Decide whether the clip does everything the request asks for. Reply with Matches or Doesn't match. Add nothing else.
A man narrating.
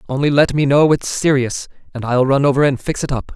Matches